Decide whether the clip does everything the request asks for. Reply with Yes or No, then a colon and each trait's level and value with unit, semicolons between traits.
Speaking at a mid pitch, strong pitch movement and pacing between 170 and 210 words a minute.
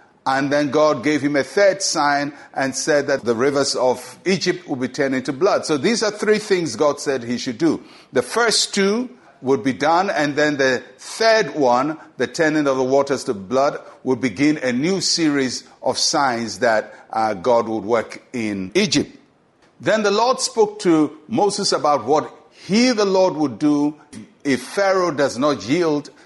Yes: medium, 150 Hz; wide, 6.0 semitones; average, 185 wpm